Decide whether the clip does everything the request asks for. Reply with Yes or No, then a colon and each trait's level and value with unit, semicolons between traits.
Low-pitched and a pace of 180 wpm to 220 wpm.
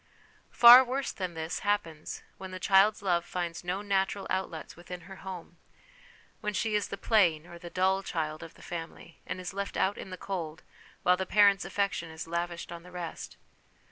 No: medium, 185 Hz; average, 190 wpm